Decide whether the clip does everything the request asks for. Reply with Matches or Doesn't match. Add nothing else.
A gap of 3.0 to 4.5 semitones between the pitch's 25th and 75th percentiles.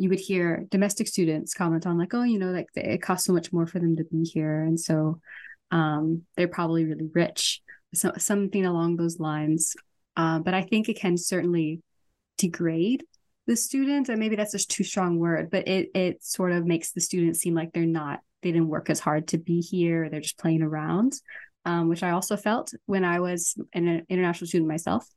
Doesn't match